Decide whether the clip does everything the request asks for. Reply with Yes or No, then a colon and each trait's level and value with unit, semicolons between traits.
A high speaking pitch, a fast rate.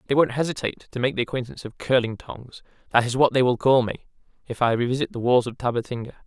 No: low, 125 Hz; fast, 210 wpm